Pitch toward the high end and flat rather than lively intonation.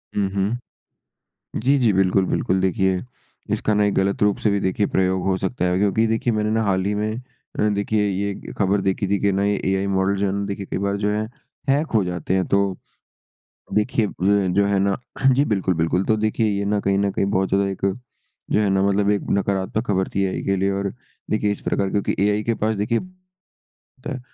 No: low, 100 Hz; narrow, 1.5 semitones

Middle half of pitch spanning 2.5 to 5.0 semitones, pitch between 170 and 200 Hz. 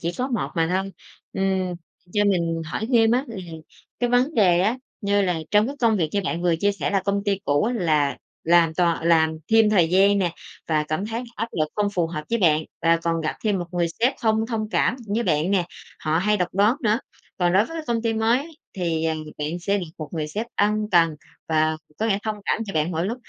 Yes: average, 4.7 semitones; high, 190 Hz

